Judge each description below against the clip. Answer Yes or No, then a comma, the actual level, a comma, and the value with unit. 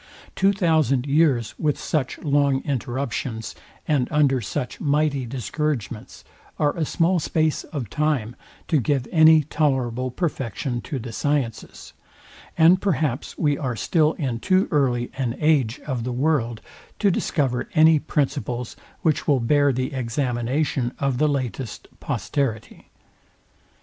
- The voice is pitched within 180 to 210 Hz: No, medium, 140 Hz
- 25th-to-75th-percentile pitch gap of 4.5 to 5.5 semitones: No, average, 3.8 semitones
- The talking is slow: Yes, slow, 130 wpm